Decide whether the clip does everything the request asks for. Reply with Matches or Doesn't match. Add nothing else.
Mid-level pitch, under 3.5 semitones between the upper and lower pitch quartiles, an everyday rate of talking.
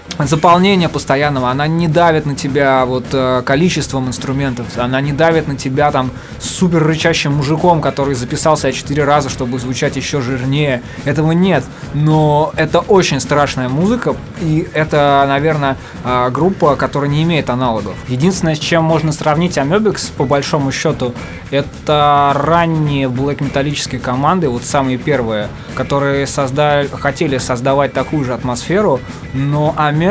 Matches